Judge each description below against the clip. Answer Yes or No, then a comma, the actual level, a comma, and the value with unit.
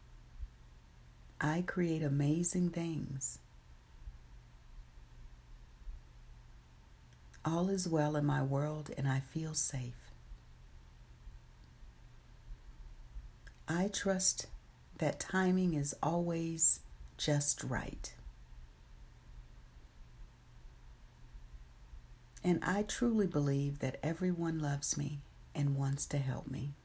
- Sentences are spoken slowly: Yes, slow, 80 wpm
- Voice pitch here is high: No, low, 135 Hz